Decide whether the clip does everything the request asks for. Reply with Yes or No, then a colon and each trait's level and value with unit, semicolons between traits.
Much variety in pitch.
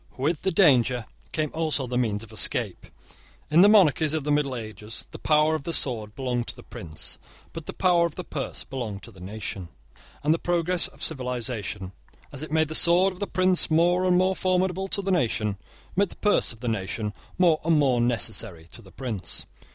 Yes: wide, 7.0 semitones